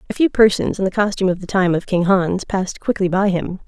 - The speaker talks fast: Yes, fast, 260 wpm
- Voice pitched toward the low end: No, high, 190 Hz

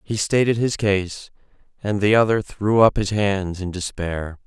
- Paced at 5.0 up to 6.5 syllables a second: No, 4.2 syllables/s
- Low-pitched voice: Yes, low, 100 Hz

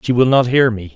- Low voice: Yes, low, 120 Hz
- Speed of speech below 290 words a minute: No, fast, 315 wpm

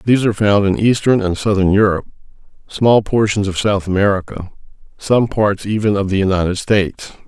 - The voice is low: Yes, low, 100 Hz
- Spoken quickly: No, average, 165 wpm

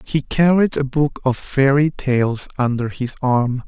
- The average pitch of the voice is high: No, low, 135 Hz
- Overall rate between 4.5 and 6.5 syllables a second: No, 3.9 syllables/s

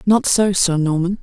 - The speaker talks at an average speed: Yes, average, 195 wpm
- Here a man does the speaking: No, female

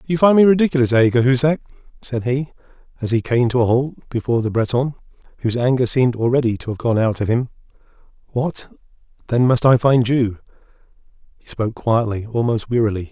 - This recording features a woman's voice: No, male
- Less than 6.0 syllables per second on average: No, 6.1 syllables/s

